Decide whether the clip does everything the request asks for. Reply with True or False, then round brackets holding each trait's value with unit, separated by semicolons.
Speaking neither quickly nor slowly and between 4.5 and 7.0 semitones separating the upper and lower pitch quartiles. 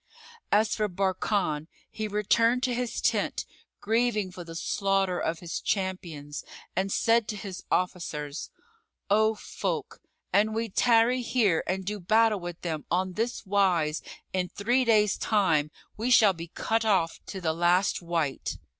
False (150 wpm; 4.0 semitones)